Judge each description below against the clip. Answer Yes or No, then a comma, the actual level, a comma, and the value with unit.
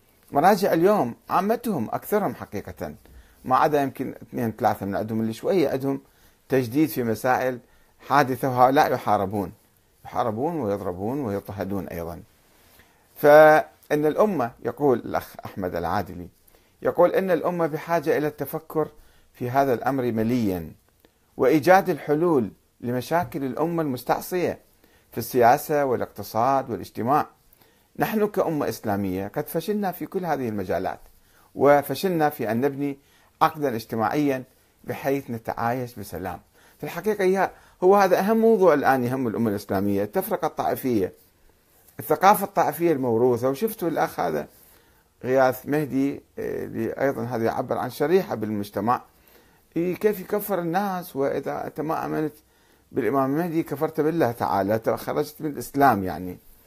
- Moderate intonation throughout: No, wide, 5.9 semitones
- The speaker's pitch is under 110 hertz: No, low, 135 Hz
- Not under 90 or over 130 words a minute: Yes, average, 120 wpm